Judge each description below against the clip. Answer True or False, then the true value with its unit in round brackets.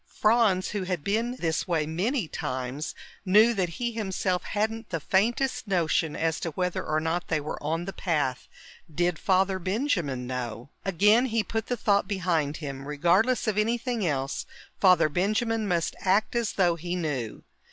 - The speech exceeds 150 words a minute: True (165 wpm)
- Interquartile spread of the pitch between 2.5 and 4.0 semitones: False (5.2 semitones)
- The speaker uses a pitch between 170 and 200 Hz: True (185 Hz)